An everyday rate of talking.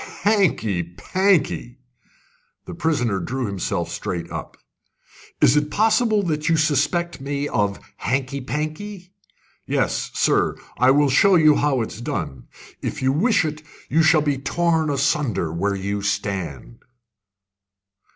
No: slow, 130 wpm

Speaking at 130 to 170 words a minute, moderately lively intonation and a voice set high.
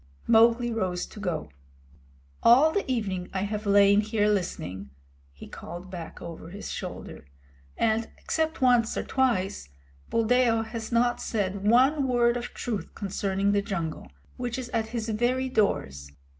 Yes: average, 145 wpm; average, 4.0 semitones; high, 220 Hz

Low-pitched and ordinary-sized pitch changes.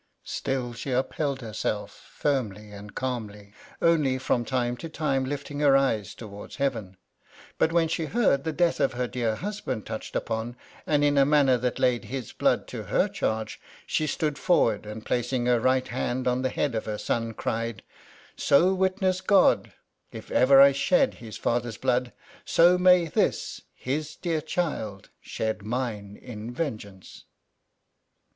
Yes: low, 130 Hz; average, 4.8 semitones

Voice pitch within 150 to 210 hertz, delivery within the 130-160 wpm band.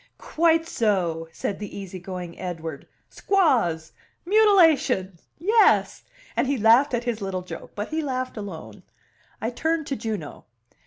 No: high, 225 Hz; average, 140 wpm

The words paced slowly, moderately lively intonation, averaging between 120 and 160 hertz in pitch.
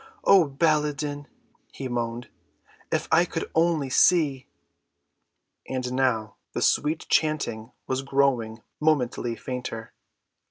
Yes: slow, 105 wpm; average, 4.0 semitones; low, 135 Hz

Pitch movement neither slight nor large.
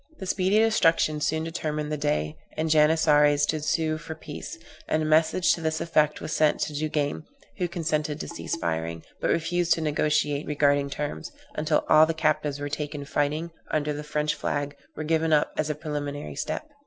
No: narrow, 1.4 semitones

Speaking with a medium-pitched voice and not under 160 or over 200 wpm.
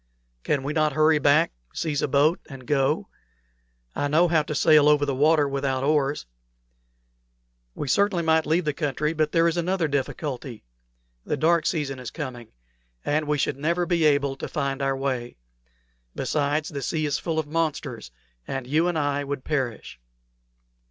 Yes: medium, 150 Hz; average, 170 wpm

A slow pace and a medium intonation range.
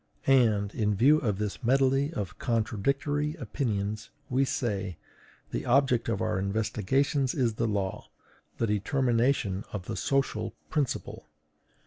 Yes: slow, 125 wpm; average, 4.7 semitones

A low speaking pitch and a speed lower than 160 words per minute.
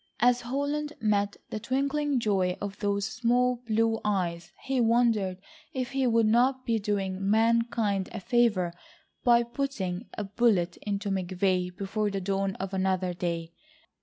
No: high, 210 Hz; average, 145 wpm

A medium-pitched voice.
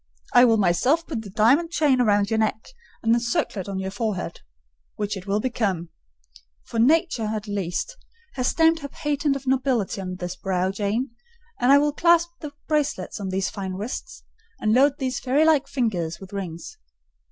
No: high, 225 Hz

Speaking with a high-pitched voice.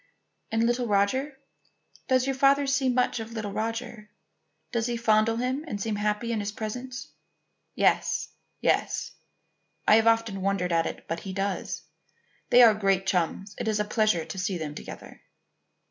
Yes: high, 220 Hz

